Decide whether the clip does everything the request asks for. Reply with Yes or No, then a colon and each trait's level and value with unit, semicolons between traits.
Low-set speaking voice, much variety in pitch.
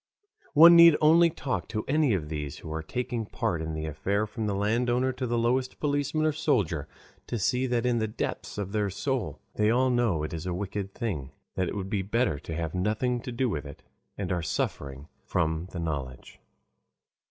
Yes: low, 105 Hz; wide, 7.2 semitones